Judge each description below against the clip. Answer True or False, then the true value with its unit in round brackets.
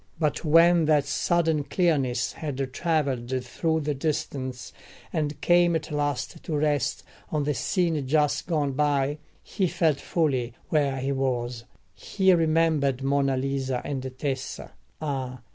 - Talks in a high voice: False (145 Hz)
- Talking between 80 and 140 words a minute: True (135 wpm)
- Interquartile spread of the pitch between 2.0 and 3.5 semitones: True (3.0 semitones)